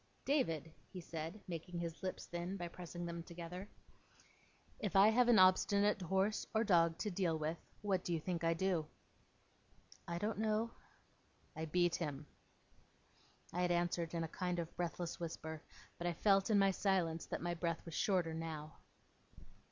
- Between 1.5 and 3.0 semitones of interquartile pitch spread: Yes, narrow, 2.6 semitones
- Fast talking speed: No, average, 165 wpm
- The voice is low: No, medium, 175 Hz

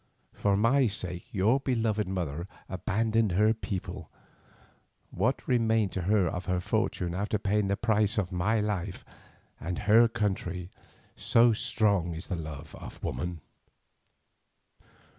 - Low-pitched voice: Yes, low, 100 Hz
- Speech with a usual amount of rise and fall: Yes, average, 3.7 semitones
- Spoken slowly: Yes, slow, 130 wpm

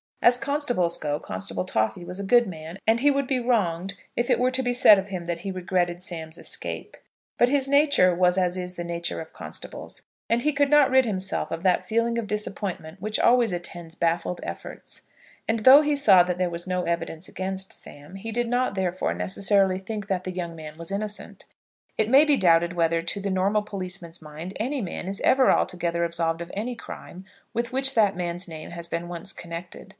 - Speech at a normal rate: No, fast, 210 wpm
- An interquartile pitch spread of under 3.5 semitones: No, average, 5.2 semitones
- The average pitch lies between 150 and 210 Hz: Yes, medium, 185 Hz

